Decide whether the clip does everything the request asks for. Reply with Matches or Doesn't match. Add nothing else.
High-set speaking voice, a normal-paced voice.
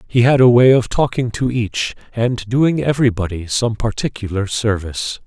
Doesn't match